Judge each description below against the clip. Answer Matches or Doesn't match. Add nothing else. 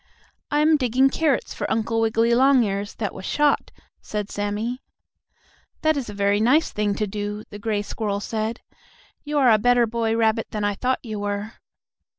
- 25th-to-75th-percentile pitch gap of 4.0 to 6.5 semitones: Doesn't match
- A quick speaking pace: Doesn't match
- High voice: Matches